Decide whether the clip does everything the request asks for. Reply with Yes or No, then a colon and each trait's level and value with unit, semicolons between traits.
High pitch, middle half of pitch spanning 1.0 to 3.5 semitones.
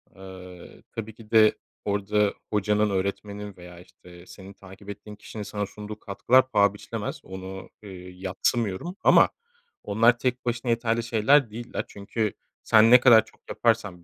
No: low, 105 Hz; average, 3.0 semitones